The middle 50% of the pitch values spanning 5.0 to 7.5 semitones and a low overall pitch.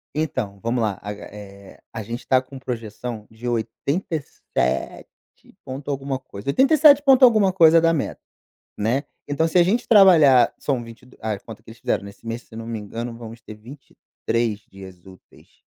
Yes: average, 5.3 semitones; low, 120 Hz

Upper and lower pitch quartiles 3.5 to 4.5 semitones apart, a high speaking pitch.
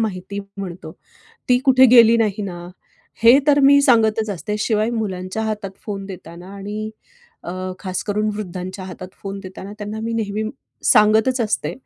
No: average, 2.8 semitones; high, 210 Hz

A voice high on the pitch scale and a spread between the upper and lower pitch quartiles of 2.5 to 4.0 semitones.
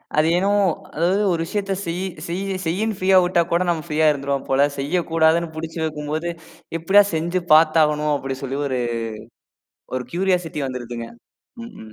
No: medium, 160 Hz; average, 3.3 semitones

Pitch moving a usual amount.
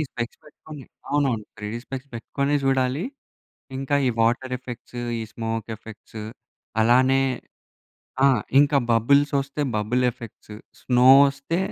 Yes: average, 3.2 semitones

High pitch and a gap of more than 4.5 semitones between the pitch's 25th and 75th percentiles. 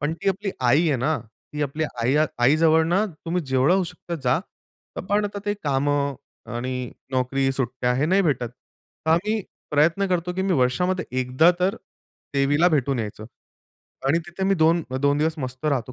No: medium, 150 Hz; average, 5.0 semitones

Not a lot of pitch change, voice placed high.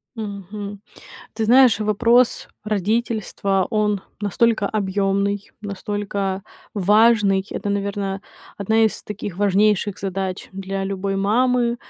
Yes: narrow, 1.8 semitones; high, 205 Hz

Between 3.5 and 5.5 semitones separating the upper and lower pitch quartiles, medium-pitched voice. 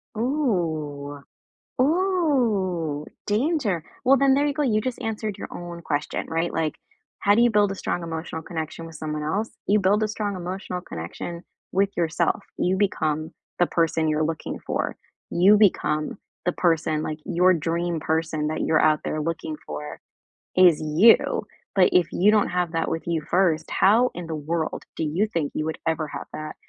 Yes: average, 4.7 semitones; medium, 170 Hz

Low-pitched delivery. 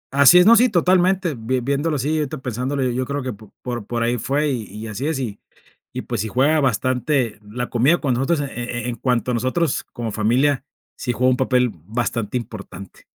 Yes: low, 125 Hz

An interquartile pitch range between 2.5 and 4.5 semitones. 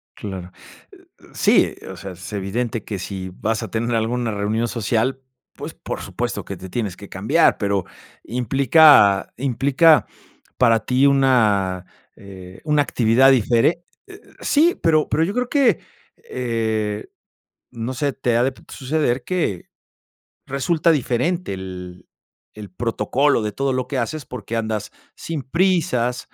No: average, 5.0 semitones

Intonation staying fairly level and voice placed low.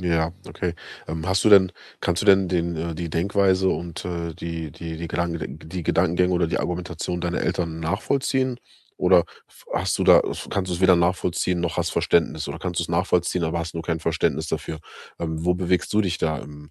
Yes: narrow, 1.8 semitones; very low, 85 Hz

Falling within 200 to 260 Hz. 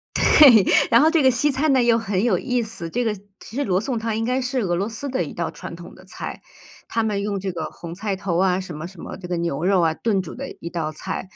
Yes: high, 205 Hz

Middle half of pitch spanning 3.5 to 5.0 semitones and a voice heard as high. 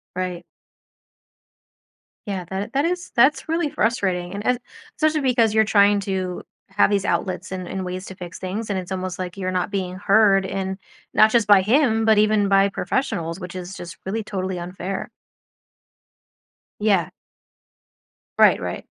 No: average, 2.8 semitones; high, 195 Hz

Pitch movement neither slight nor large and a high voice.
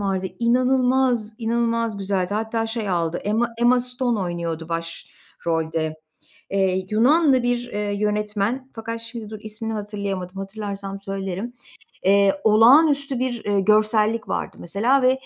Yes: average, 3.5 semitones; high, 215 Hz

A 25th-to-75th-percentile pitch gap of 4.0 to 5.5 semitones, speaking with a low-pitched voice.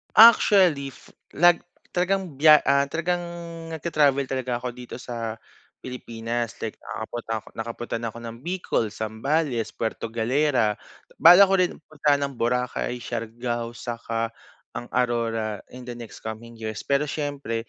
Yes: average, 4.3 semitones; low, 125 Hz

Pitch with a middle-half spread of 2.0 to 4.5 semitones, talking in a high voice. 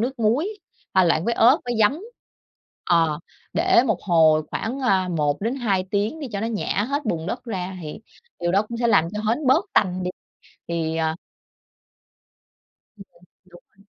No: wide, 5.5 semitones; high, 200 Hz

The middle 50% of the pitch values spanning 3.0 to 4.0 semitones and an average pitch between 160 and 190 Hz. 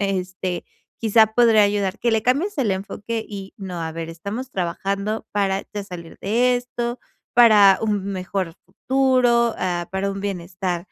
No: average, 3.7 semitones; high, 200 Hz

